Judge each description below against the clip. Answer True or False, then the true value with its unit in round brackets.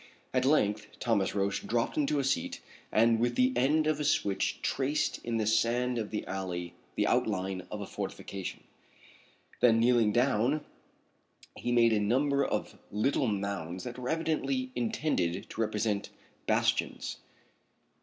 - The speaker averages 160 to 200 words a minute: False (145 wpm)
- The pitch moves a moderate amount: True (4.6 semitones)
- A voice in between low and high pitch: False (115 Hz)